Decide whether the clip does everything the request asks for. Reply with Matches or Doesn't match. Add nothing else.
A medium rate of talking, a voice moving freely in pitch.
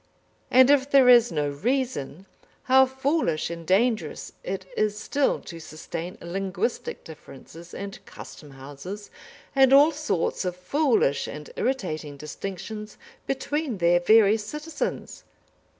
Doesn't match